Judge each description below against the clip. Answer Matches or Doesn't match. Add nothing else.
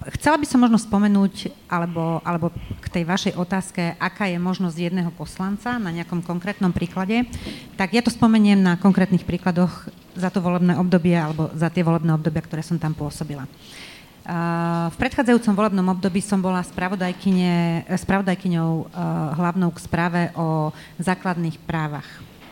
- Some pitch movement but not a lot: Doesn't match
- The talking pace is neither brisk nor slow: Matches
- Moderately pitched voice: Matches